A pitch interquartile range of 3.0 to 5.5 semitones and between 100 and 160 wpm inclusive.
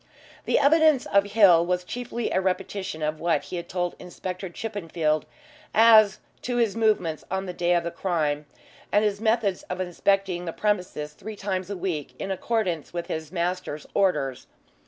No: average, 3.3 semitones; average, 170 wpm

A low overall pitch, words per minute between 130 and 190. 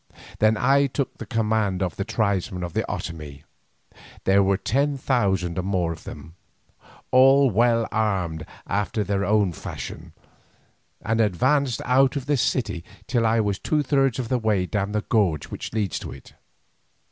Yes: low, 105 Hz; average, 155 wpm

